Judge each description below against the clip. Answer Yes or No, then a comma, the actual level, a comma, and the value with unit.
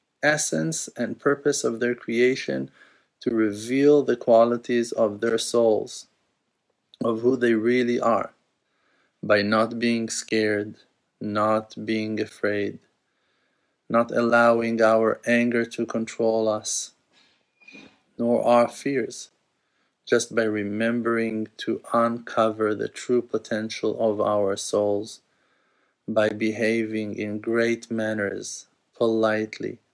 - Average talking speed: No, slow, 105 wpm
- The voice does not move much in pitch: Yes, narrow, 1.4 semitones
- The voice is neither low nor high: No, low, 115 Hz